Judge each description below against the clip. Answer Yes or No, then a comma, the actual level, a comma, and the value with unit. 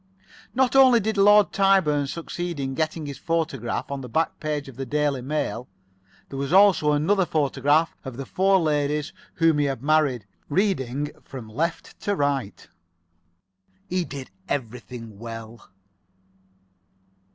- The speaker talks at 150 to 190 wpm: No, average, 140 wpm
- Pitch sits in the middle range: Yes, medium, 150 Hz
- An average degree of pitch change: Yes, average, 4.2 semitones